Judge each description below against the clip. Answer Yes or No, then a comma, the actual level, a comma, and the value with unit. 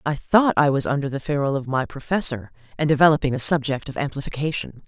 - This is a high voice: No, medium, 140 Hz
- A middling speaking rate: Yes, average, 195 wpm